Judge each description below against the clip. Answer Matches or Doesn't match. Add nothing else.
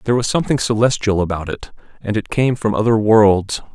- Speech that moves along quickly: Doesn't match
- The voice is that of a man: Matches